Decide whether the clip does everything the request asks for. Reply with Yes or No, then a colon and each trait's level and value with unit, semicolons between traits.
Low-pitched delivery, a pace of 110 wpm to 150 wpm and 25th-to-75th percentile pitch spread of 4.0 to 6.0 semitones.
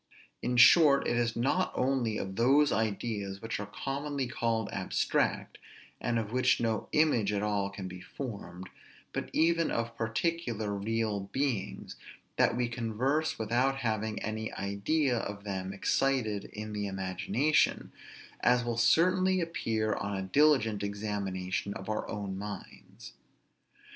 Yes: low, 110 Hz; average, 140 wpm; average, 4.5 semitones